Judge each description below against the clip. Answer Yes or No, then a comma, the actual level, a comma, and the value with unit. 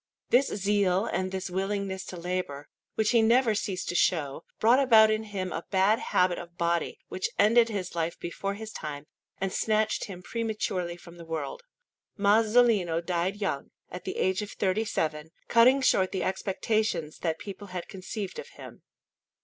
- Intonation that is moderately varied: Yes, average, 3.6 semitones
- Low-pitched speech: No, high, 190 Hz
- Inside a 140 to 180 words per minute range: Yes, average, 170 wpm